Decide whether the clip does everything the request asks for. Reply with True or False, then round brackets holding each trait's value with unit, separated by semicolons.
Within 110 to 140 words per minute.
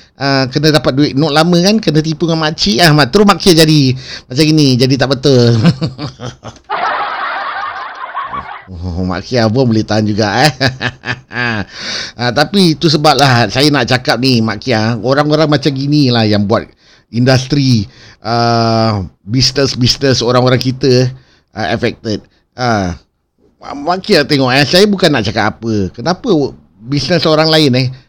False (150 wpm)